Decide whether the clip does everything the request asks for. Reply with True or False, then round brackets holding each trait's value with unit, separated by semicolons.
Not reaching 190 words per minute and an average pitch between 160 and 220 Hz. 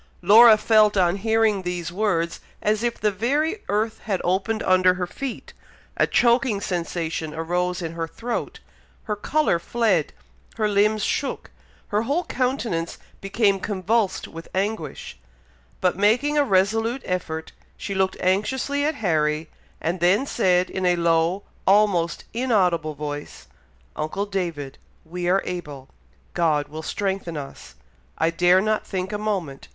True (140 wpm; 190 Hz)